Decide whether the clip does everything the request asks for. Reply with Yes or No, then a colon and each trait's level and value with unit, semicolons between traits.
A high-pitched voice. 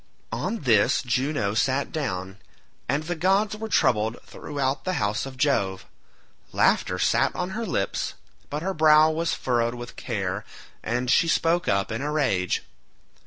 No: medium, 140 Hz